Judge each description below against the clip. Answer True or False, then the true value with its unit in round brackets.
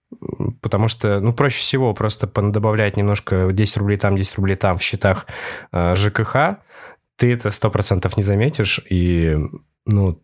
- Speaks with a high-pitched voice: False (105 Hz)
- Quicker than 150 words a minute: False (140 wpm)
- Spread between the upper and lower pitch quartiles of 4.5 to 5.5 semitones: False (2.9 semitones)